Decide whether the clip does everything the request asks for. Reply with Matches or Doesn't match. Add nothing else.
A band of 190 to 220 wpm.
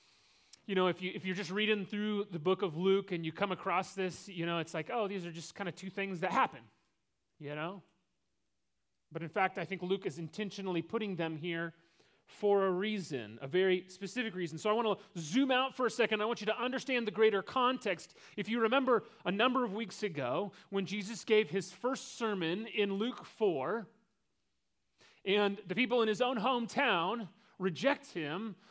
Matches